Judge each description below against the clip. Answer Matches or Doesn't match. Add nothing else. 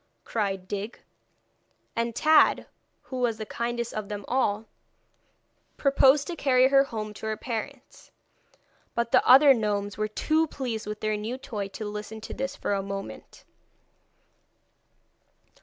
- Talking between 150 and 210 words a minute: Doesn't match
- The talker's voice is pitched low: Doesn't match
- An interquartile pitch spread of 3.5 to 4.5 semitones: Matches